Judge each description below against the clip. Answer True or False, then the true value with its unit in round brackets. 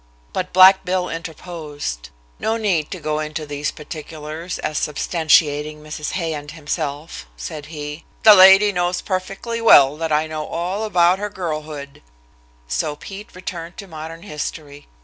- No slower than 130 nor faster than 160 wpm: True (150 wpm)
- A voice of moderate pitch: True (160 Hz)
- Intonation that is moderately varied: True (3.5 semitones)